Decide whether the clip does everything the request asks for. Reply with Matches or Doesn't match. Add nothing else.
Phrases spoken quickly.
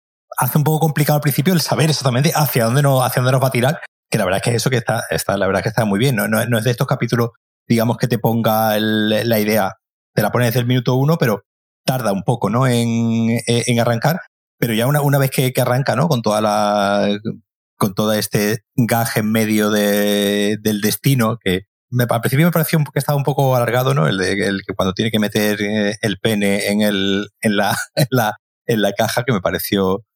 Matches